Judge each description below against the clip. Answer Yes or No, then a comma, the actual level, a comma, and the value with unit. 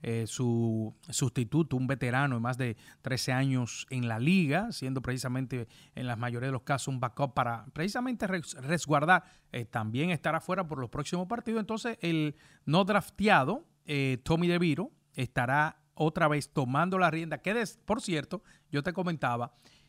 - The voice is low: No, medium, 145 Hz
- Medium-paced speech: Yes, average, 165 wpm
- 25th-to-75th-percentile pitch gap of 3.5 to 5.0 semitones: No, wide, 5.5 semitones